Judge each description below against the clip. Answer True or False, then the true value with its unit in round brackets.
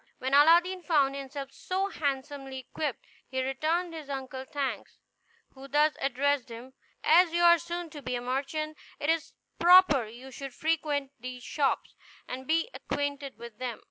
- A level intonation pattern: False (3.3 semitones)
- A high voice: True (280 Hz)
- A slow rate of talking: False (160 wpm)